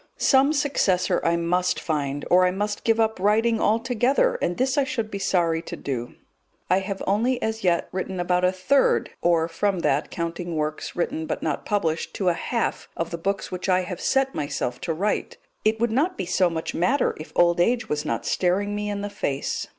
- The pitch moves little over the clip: No, average, 4.6 semitones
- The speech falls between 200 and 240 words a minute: Yes, fast, 205 wpm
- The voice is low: No, medium, 185 Hz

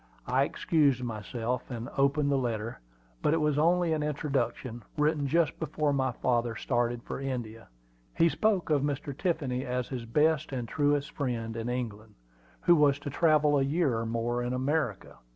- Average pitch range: Yes, average, 3.8 semitones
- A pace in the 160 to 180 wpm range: Yes, average, 170 wpm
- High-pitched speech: No, low, 135 Hz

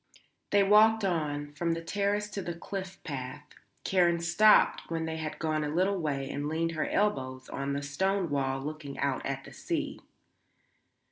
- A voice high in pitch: No, medium, 160 Hz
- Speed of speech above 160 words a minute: Yes, average, 175 wpm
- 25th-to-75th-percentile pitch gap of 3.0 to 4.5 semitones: No, average, 5.2 semitones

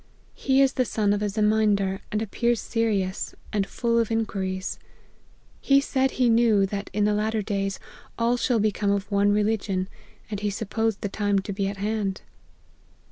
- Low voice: No, high, 210 Hz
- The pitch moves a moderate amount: No, narrow, 2.1 semitones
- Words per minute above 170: Yes, average, 180 wpm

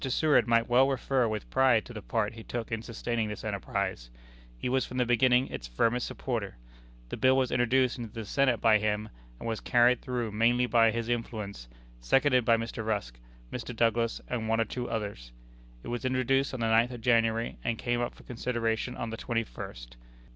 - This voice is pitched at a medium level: No, low, 115 Hz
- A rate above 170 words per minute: Yes, average, 200 wpm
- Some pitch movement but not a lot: No, narrow, 1.9 semitones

